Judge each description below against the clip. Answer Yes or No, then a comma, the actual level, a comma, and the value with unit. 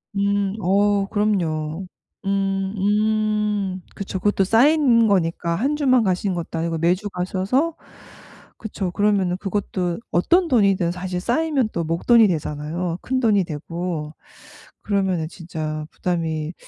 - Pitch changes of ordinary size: Yes, average, 3.6 semitones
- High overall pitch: Yes, high, 195 Hz